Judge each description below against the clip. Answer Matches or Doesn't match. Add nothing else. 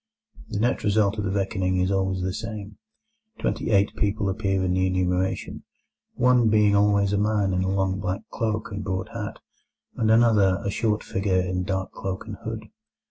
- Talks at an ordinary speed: Matches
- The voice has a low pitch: Matches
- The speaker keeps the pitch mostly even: Matches